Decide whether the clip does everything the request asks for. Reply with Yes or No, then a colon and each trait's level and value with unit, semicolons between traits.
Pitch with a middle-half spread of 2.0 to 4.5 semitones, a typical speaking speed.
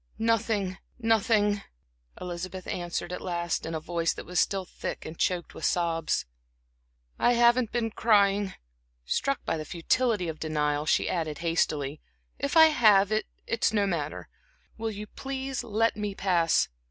No: average, 5.0 semitones; average, 155 wpm